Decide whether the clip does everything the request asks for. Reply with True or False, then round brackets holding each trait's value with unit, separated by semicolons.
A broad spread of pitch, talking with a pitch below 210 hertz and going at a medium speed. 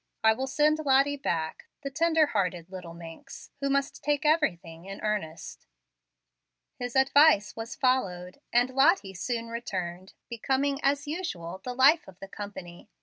False (7.2 semitones; 240 Hz; 145 wpm)